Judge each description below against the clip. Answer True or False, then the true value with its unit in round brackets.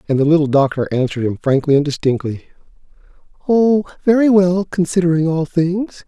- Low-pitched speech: False (165 Hz)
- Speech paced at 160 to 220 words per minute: False (150 wpm)